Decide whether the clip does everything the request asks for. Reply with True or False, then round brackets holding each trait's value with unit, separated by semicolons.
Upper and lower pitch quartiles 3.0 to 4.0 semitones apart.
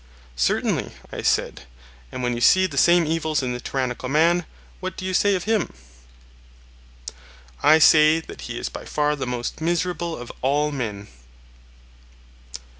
False (5.3 semitones)